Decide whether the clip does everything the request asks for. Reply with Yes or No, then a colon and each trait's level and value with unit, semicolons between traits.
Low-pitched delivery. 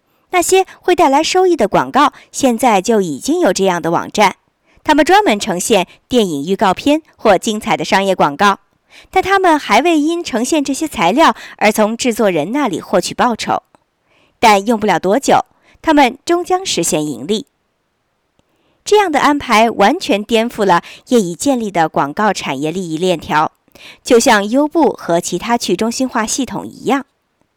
No: high, 230 Hz